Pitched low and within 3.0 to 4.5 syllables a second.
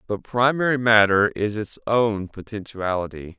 Yes: low, 110 Hz; 4.4 syllables/s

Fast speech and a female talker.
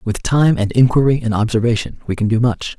No: fast, 215 wpm; male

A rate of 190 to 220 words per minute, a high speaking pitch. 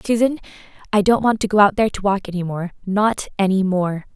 Yes: average, 200 wpm; high, 200 Hz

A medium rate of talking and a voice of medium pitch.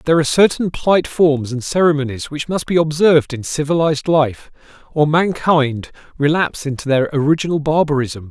Yes: average, 150 wpm; medium, 150 Hz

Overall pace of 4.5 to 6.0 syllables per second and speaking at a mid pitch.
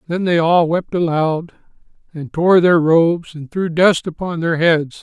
No: 4.3 syllables/s; medium, 165 Hz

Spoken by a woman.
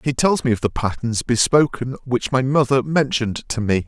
No: male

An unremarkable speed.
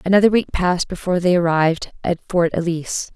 Yes: average, 170 wpm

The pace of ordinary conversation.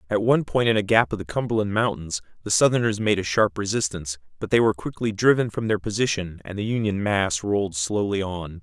No: fast, 215 wpm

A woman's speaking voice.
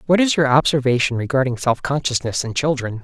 No: male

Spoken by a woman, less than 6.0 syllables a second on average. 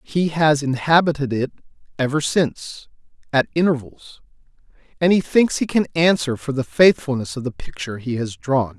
No: male; 5.1 syllables/s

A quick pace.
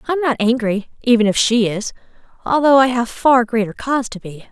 Yes: fast, 215 wpm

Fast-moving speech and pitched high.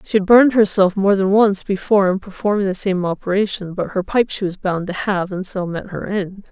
Yes: fast, 240 wpm; high, 195 Hz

